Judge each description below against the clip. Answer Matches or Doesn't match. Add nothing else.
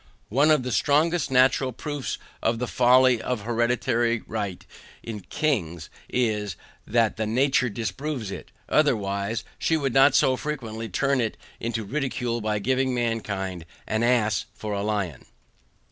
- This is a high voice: Doesn't match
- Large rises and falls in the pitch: Doesn't match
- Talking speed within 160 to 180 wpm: Doesn't match